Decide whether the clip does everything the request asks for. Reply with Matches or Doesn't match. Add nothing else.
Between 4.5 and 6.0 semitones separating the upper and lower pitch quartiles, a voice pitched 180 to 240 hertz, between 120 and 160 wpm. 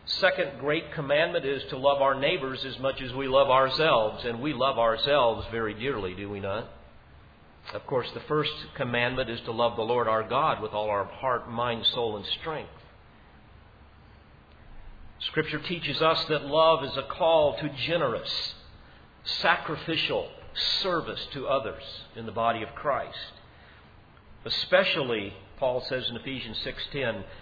Doesn't match